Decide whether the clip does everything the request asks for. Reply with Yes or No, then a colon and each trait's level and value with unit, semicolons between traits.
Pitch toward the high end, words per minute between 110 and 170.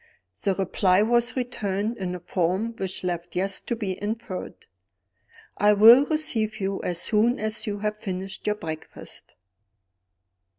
Yes: high, 205 Hz; average, 140 wpm